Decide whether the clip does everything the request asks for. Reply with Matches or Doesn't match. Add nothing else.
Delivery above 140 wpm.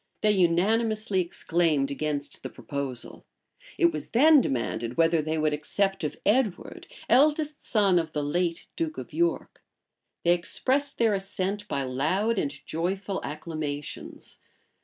Doesn't match